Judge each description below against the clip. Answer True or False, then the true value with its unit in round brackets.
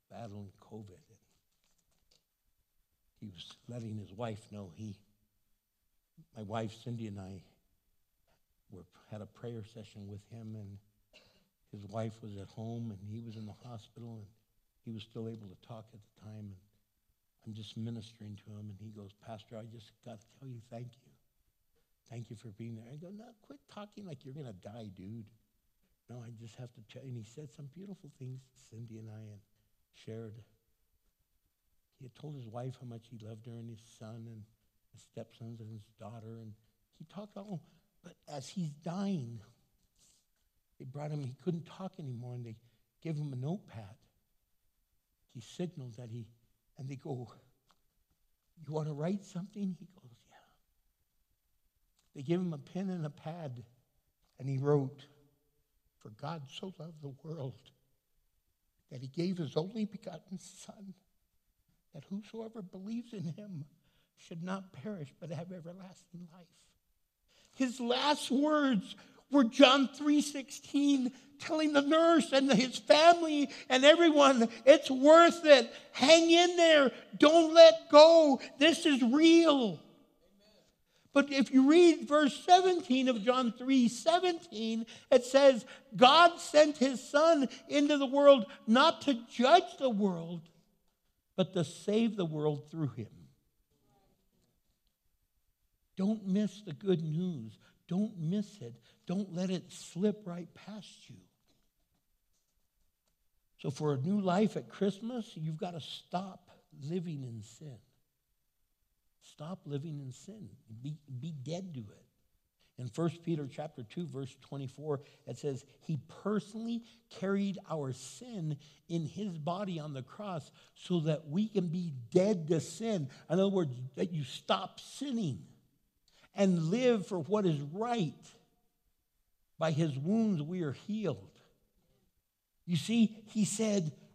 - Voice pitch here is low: False (155 Hz)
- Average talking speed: True (150 wpm)